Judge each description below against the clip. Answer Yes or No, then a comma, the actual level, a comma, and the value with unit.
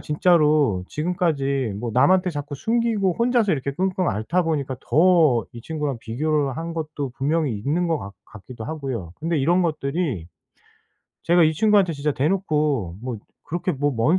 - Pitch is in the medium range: Yes, medium, 150 Hz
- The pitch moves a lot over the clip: No, average, 4.7 semitones